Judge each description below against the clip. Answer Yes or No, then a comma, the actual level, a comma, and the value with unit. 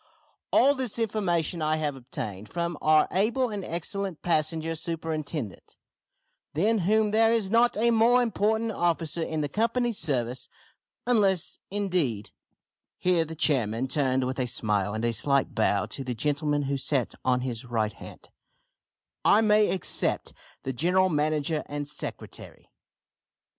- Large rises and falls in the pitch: Yes, wide, 7.4 semitones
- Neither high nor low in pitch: Yes, medium, 160 Hz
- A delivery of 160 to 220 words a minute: No, average, 140 wpm